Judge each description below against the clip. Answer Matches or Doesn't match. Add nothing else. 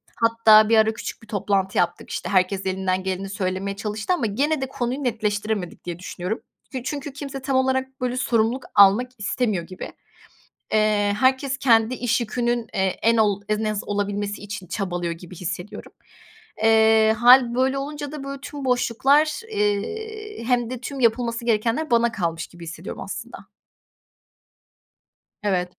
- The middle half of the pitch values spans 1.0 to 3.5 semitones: Doesn't match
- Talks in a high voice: Matches